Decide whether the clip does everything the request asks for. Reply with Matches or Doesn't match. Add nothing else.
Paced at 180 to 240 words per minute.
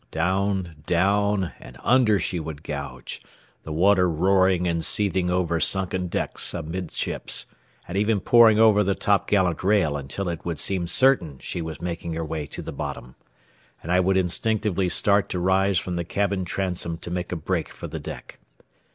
Doesn't match